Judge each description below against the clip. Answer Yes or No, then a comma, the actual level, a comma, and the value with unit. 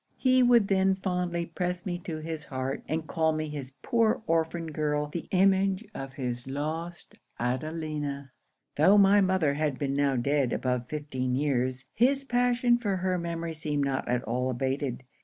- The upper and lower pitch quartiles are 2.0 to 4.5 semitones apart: No, average, 5.3 semitones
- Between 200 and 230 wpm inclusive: No, average, 165 wpm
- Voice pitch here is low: No, medium, 155 Hz